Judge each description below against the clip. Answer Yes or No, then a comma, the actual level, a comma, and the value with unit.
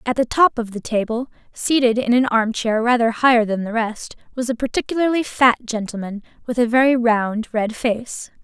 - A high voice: Yes, high, 235 Hz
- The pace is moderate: Yes, average, 190 wpm